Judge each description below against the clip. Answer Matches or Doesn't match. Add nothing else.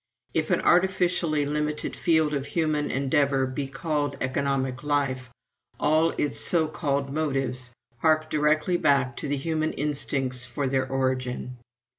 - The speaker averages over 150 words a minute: Doesn't match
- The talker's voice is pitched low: Doesn't match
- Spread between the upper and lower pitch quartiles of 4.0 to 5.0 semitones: Doesn't match